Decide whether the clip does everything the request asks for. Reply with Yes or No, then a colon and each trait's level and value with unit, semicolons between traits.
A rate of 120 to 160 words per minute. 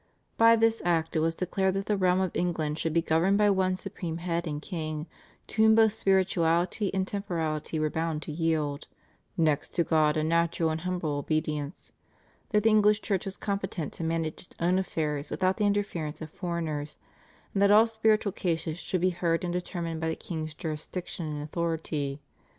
No: average, 185 wpm